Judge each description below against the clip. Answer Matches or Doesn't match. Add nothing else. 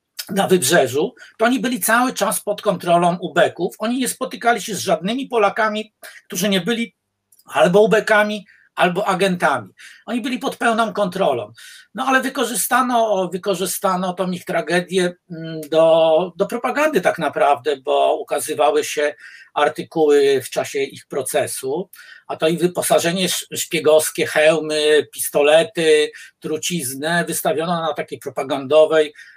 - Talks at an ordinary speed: Matches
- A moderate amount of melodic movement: Doesn't match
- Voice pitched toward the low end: Doesn't match